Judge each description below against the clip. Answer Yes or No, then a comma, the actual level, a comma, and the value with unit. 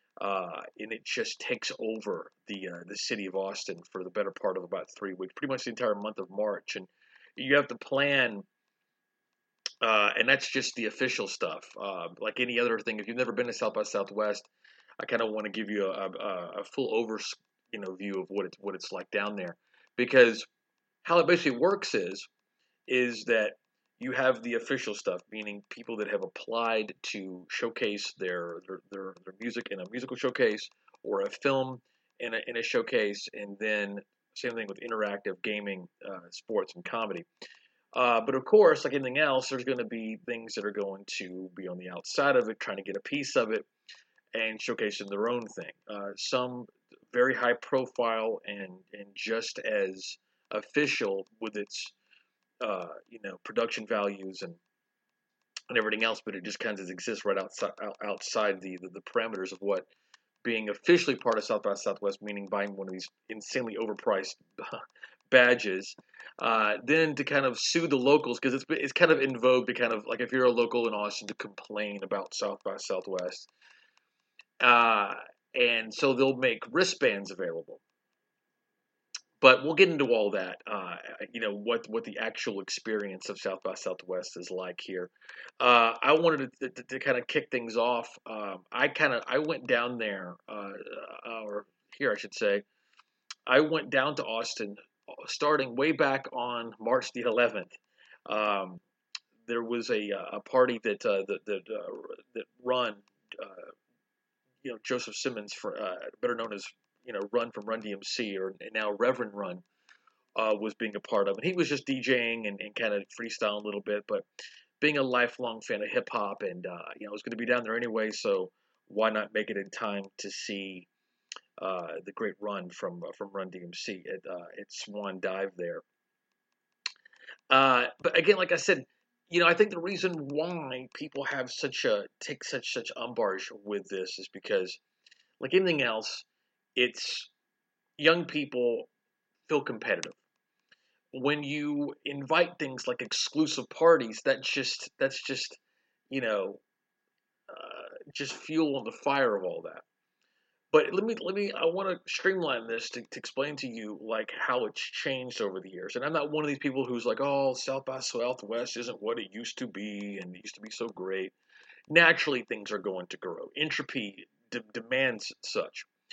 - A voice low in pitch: Yes, low, 120 Hz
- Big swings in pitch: Yes, wide, 7.0 semitones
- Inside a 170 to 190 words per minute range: Yes, average, 185 wpm